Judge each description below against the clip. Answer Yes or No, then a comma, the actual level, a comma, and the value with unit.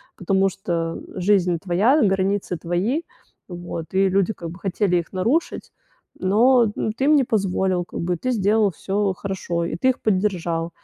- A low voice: No, high, 190 Hz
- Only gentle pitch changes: No, average, 3.2 semitones